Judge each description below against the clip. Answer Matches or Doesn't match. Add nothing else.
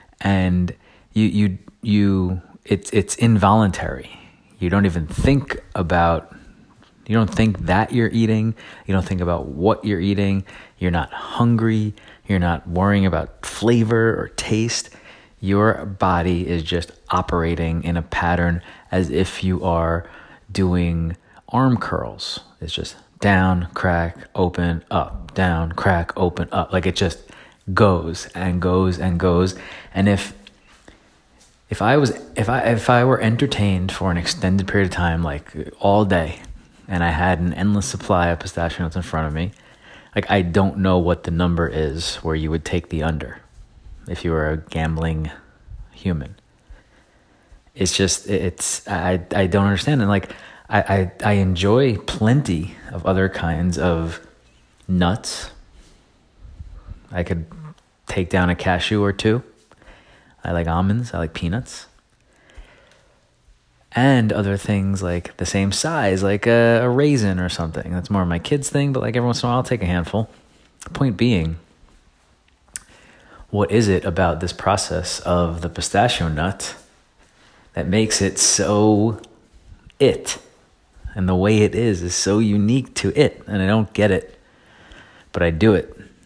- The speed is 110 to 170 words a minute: Matches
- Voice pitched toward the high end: Doesn't match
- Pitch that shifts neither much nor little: Matches